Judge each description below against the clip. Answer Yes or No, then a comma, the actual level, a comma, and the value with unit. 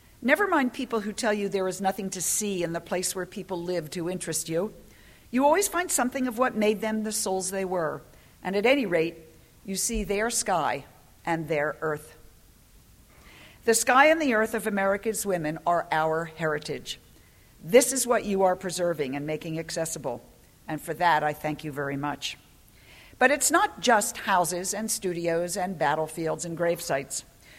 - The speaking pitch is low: No, medium, 185 Hz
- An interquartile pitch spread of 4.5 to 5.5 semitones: Yes, average, 5.1 semitones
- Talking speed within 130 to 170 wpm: No, average, 180 wpm